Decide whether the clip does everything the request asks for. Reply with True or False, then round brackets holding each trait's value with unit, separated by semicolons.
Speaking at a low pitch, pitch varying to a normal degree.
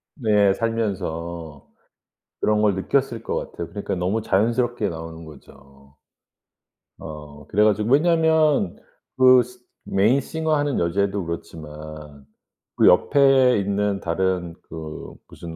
False (100 Hz; 6.6 semitones)